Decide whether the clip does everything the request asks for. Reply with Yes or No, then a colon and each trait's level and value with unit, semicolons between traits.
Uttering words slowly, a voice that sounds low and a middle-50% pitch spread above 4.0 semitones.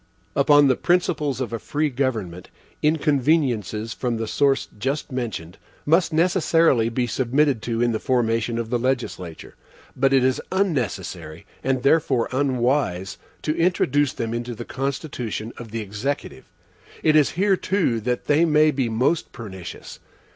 No: average, 145 wpm; low, 130 Hz; average, 4.4 semitones